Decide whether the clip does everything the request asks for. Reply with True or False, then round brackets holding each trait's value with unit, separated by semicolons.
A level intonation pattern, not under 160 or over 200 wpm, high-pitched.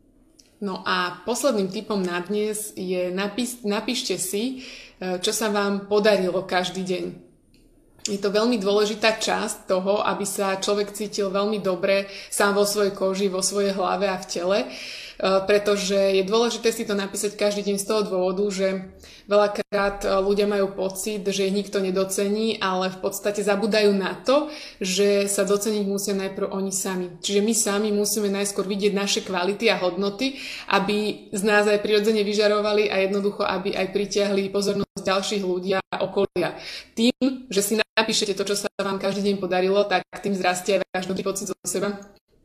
True (1.4 semitones; 165 wpm; 200 Hz)